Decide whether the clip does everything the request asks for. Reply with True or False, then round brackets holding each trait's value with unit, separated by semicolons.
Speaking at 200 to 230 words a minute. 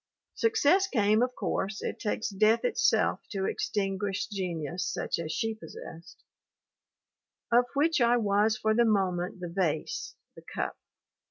False (140 wpm)